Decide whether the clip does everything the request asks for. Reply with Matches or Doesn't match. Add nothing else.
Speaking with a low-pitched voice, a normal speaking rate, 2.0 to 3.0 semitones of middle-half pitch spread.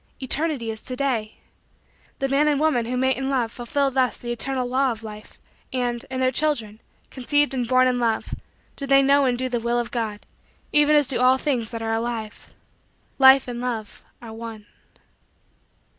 Doesn't match